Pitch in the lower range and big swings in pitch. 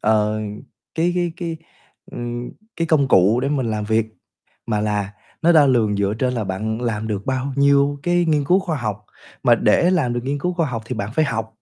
Yes: low, 125 Hz; wide, 6.0 semitones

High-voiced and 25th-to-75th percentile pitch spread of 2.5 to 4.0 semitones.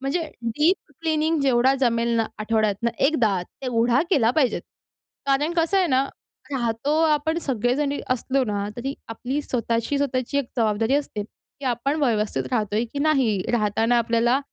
Yes: very high, 250 Hz; average, 3.7 semitones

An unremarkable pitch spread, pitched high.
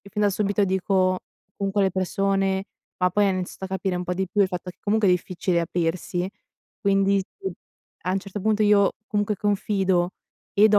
No: narrow, 1.7 semitones; high, 195 Hz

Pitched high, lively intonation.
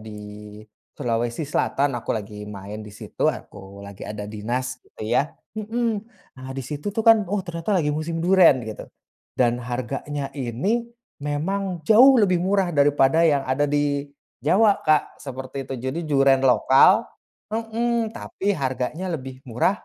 No: medium, 145 Hz; wide, 7.2 semitones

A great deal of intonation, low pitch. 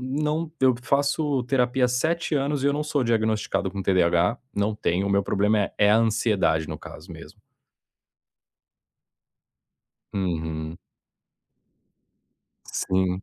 Yes: wide, 6.0 semitones; low, 110 Hz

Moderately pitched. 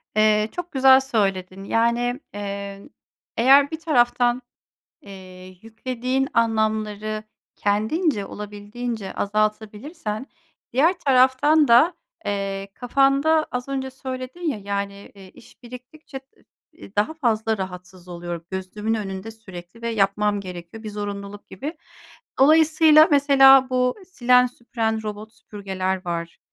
No: high, 225 Hz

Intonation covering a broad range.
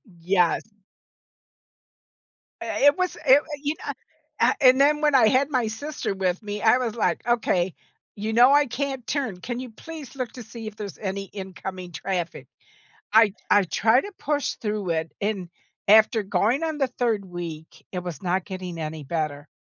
Yes: wide, 5.8 semitones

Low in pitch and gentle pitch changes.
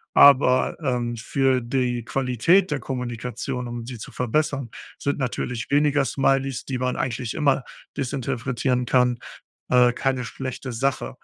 Yes: low, 125 Hz; narrow, 1.9 semitones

